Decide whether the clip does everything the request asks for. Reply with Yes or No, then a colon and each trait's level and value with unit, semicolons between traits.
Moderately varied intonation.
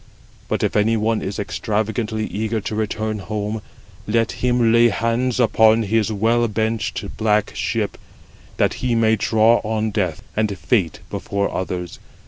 No: narrow, 1.4 semitones